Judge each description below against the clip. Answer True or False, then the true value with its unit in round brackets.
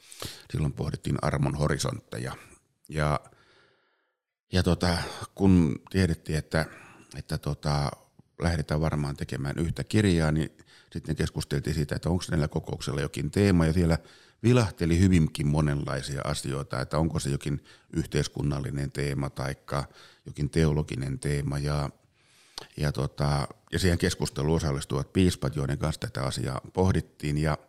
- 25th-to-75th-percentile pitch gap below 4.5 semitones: True (2.9 semitones)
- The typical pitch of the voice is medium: False (75 Hz)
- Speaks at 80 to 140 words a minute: True (125 wpm)